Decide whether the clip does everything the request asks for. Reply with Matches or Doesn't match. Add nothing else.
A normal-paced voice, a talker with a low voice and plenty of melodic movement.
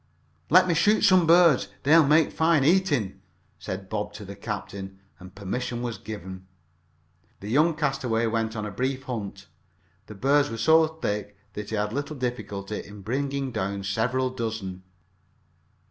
Matches